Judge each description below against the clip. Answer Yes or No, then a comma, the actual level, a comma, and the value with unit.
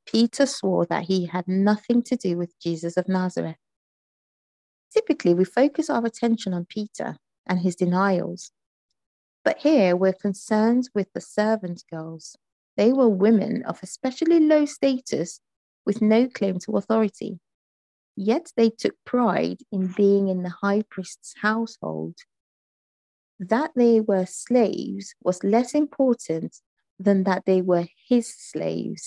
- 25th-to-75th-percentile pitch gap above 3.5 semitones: Yes, average, 4.5 semitones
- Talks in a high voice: Yes, high, 205 Hz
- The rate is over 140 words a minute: No, slow, 135 wpm